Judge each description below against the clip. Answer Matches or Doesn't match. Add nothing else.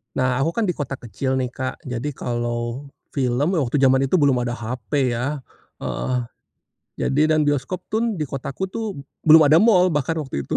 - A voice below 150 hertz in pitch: Matches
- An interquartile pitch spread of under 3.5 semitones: Doesn't match